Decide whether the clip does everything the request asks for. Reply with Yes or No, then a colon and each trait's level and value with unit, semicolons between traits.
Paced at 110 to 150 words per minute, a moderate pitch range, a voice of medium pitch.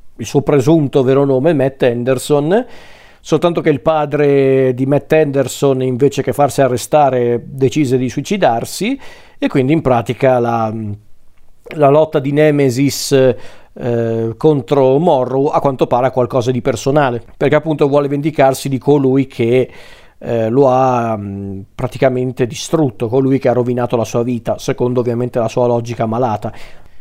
No: average, 145 wpm; average, 3.0 semitones; low, 130 Hz